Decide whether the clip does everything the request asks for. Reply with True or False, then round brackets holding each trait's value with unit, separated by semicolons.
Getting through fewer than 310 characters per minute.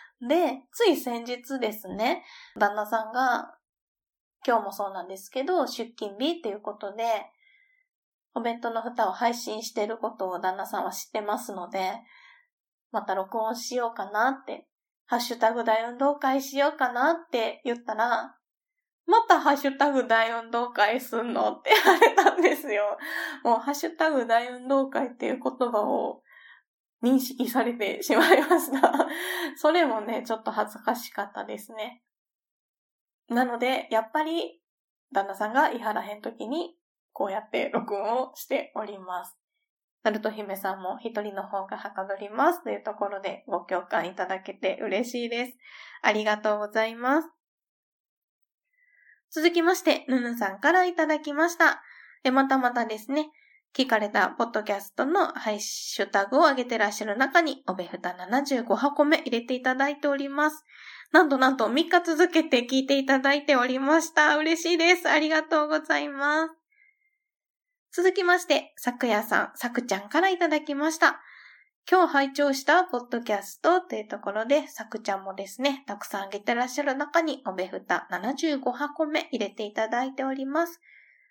False (325 characters per minute)